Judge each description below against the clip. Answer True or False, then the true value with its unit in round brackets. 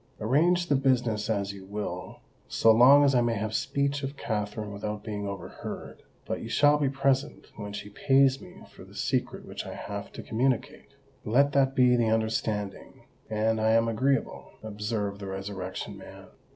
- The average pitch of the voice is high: False (110 Hz)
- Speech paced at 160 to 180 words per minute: True (175 wpm)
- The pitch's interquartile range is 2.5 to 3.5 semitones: False (4.6 semitones)